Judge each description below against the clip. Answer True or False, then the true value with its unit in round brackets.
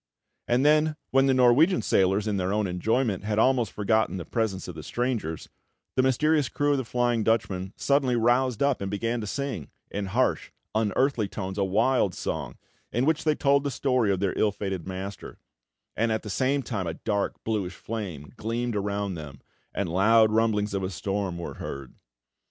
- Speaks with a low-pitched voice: True (110 Hz)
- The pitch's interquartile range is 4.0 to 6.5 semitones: True (4.6 semitones)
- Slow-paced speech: False (185 wpm)